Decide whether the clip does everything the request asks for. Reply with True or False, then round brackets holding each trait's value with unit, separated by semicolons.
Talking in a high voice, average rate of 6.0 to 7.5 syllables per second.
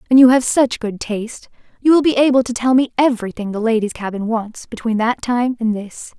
False (235 Hz; 5.6 syllables/s)